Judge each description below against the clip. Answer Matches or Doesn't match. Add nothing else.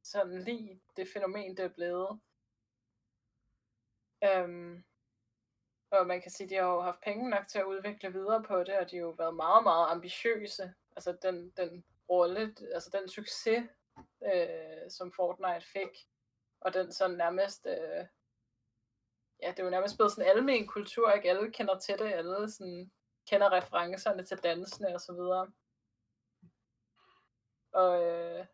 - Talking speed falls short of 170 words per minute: Matches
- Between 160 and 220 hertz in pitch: Matches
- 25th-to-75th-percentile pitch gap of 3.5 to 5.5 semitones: Doesn't match